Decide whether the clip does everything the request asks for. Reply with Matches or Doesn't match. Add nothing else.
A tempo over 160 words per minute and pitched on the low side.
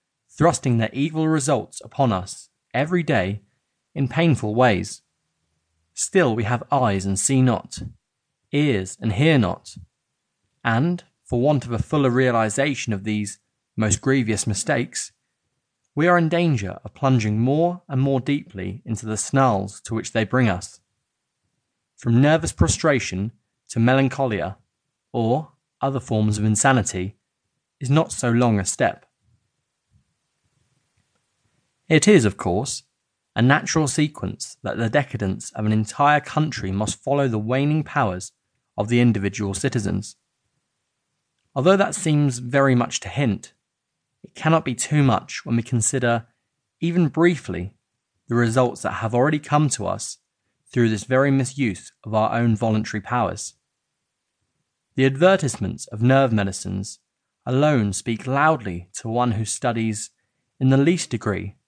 Doesn't match